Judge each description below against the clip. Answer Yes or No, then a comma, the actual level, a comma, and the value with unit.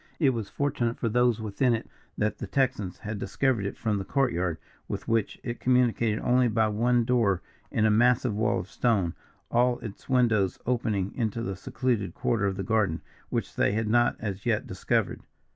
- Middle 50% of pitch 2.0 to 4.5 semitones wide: Yes, average, 3.2 semitones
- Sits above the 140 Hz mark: No, low, 115 Hz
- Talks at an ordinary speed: Yes, average, 190 wpm